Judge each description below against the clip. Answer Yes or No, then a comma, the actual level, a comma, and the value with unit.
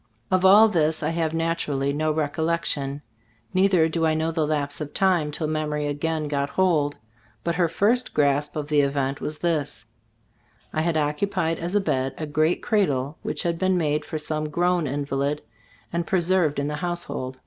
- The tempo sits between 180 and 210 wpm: Yes, average, 185 wpm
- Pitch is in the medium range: Yes, medium, 155 Hz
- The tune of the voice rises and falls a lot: No, average, 2.8 semitones